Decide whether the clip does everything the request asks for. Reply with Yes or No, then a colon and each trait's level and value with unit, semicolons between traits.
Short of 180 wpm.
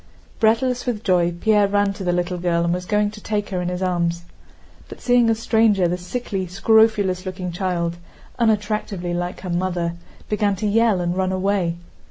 No: average, 185 wpm